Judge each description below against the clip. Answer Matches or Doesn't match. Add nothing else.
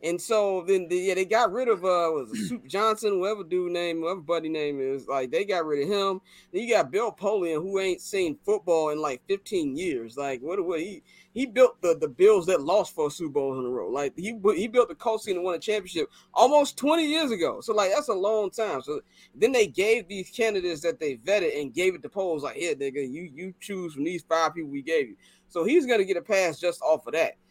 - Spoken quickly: Matches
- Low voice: Doesn't match